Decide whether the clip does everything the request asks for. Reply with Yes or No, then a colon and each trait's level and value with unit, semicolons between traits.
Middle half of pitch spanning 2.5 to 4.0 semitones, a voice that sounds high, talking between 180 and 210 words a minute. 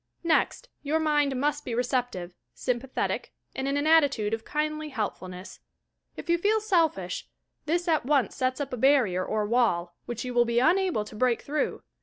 No: average, 5.0 semitones; very high, 265 Hz; average, 185 wpm